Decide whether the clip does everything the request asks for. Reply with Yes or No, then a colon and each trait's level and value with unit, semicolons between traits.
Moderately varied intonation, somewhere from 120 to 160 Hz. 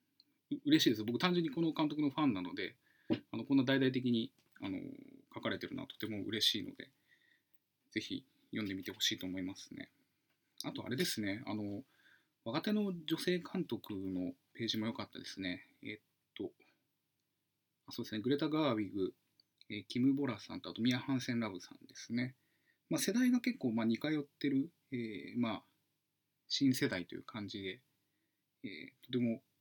No: wide, 6.3 semitones; low, 130 Hz